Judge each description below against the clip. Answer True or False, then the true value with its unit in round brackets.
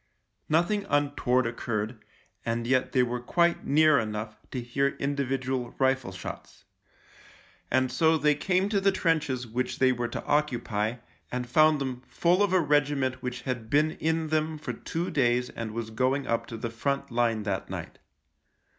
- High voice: False (130 Hz)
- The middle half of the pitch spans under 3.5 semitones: False (4.2 semitones)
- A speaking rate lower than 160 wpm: False (165 wpm)